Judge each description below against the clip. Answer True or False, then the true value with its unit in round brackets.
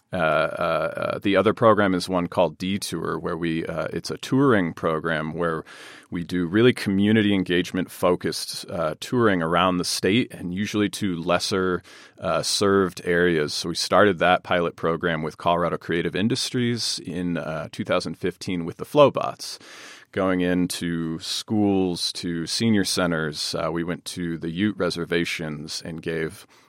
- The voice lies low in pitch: True (90 Hz)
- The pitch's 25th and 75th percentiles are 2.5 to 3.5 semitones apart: True (2.8 semitones)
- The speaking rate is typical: True (150 wpm)